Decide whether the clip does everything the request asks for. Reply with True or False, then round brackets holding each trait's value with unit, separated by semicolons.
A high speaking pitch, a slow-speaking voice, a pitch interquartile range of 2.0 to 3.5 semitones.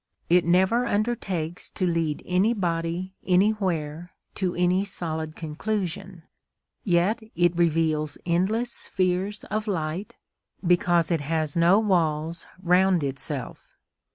False (175 Hz; 105 wpm; 2.9 semitones)